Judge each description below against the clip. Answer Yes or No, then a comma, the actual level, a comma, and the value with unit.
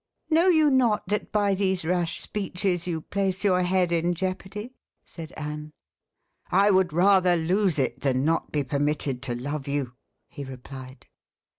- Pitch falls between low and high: Yes, medium, 175 Hz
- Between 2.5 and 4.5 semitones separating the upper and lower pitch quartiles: No, average, 5.0 semitones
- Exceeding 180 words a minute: No, average, 155 wpm